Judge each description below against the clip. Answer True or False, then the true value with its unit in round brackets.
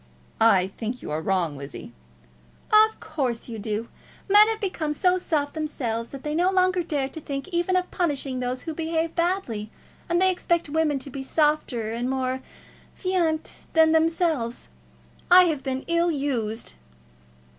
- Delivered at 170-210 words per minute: False (160 wpm)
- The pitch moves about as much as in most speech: False (5.7 semitones)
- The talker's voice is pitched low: False (300 Hz)